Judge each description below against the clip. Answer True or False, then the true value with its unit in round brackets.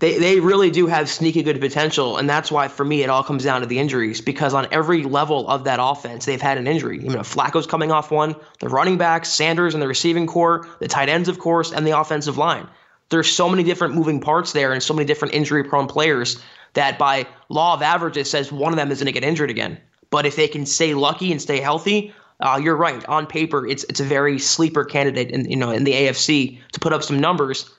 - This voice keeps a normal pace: False (245 wpm)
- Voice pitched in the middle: True (150 Hz)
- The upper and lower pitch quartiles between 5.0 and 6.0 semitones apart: False (2.7 semitones)